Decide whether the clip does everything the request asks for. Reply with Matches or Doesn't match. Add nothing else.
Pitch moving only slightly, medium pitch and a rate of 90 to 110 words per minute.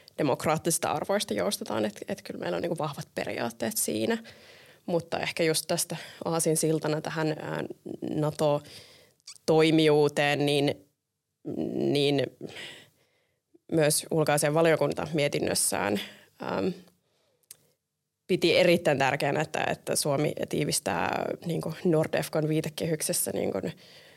Matches